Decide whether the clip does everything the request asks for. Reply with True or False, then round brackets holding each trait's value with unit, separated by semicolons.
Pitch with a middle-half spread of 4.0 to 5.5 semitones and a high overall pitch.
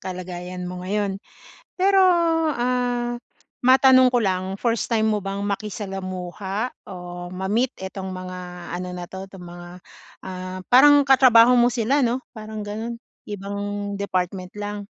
True (4.6 semitones; 205 Hz)